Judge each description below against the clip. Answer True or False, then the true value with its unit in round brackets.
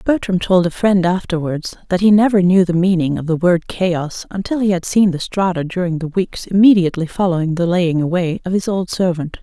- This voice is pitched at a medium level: True (180 Hz)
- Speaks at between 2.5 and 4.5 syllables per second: False (5.4 syllables/s)